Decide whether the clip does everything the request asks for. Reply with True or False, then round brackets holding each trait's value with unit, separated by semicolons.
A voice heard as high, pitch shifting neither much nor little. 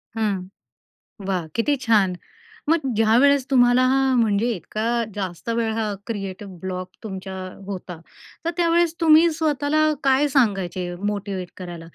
False (220 Hz; 6.0 semitones)